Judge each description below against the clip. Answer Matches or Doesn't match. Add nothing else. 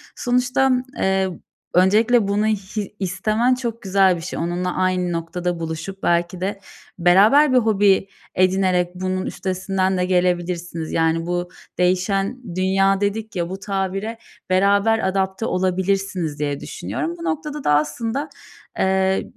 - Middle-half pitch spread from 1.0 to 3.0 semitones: Matches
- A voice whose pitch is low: Doesn't match